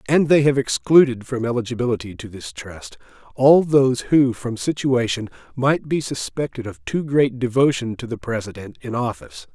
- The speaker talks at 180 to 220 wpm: No, average, 165 wpm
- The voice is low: Yes, low, 125 Hz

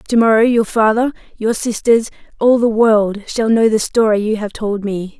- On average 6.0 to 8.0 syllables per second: No, 4.7 syllables/s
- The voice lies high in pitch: Yes, high, 220 Hz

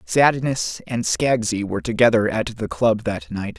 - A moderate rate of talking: Yes, average, 165 wpm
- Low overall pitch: Yes, low, 110 Hz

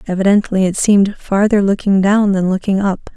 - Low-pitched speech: No, high, 195 Hz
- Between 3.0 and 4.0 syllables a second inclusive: No, 5.4 syllables/s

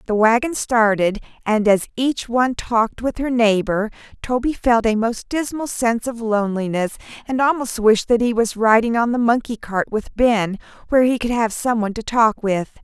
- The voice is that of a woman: Yes, female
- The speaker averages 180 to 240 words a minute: Yes, average, 190 wpm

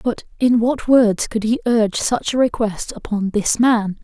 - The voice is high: Yes, high, 225 Hz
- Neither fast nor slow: Yes, average, 195 wpm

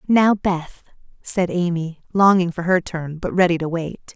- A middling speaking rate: Yes, average, 175 wpm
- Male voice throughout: No, female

